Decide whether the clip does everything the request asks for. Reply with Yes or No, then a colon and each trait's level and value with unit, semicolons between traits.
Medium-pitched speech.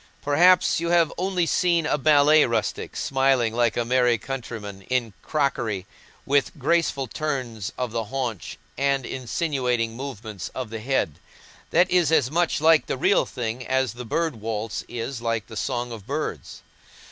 No: low, 130 Hz